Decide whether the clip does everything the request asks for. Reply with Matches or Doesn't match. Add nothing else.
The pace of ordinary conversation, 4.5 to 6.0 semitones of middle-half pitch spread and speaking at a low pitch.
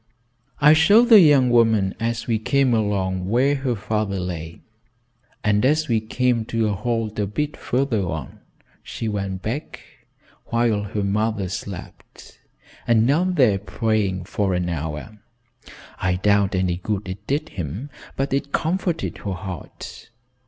Matches